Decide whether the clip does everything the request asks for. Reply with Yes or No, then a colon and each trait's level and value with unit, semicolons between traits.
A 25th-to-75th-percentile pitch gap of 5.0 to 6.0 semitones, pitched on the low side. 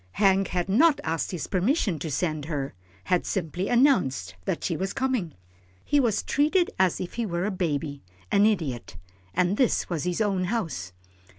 No: average, 5.3 semitones; medium, 185 Hz